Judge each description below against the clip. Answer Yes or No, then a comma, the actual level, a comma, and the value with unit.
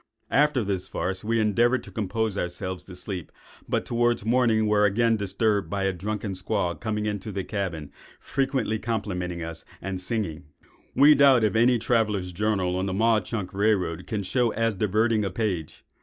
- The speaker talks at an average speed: Yes, average, 175 wpm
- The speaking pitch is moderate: No, low, 105 Hz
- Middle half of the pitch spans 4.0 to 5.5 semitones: No, average, 3.4 semitones